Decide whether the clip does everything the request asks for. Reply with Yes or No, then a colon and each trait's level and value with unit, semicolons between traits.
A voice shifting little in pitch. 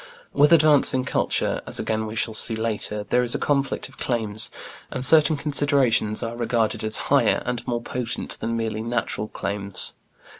No: average, 3.5 semitones